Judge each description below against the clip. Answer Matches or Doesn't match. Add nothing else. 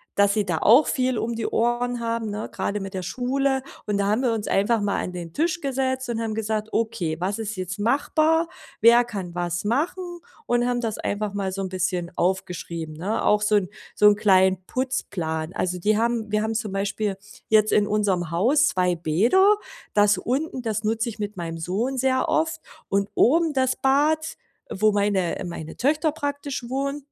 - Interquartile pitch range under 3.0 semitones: Doesn't match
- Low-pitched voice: Doesn't match